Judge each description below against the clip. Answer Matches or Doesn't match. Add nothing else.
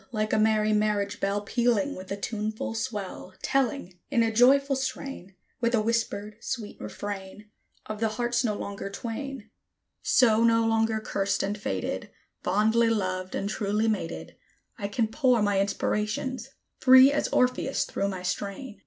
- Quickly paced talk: Doesn't match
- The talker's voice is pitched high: Matches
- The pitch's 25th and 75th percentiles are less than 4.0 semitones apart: Matches